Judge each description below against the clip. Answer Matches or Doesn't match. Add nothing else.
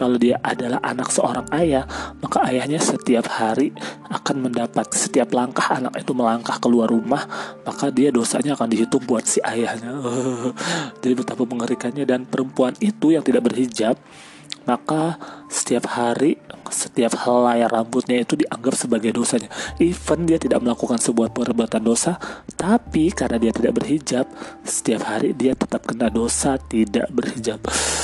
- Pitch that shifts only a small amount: Matches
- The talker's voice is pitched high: Doesn't match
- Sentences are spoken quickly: Matches